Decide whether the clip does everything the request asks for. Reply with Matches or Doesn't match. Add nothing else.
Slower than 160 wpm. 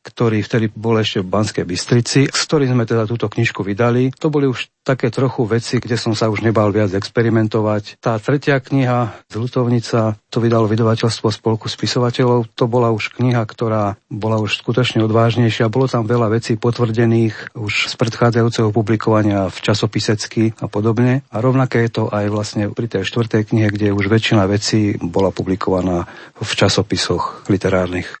Doesn't match